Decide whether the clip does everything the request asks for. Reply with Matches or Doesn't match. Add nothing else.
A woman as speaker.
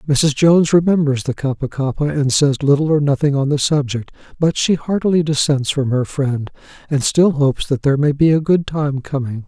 Doesn't match